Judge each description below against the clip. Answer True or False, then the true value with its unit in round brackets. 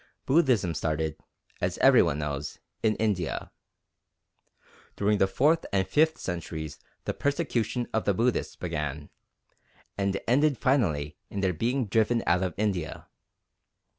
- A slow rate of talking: True (130 wpm)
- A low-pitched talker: True (100 Hz)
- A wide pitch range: True (7.1 semitones)